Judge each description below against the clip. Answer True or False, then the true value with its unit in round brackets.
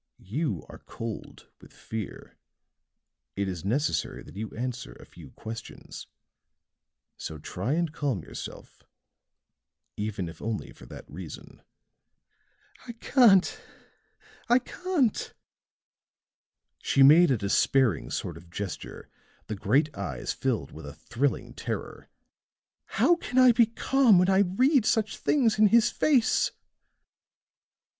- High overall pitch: False (135 Hz)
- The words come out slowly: True (120 wpm)